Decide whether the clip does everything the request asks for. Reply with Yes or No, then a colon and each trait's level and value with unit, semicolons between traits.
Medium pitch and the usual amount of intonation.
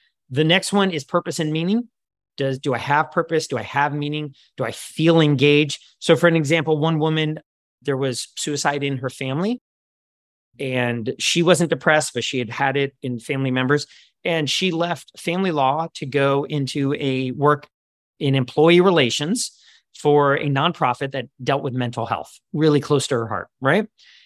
Yes: medium, 145 Hz; average, 3.2 semitones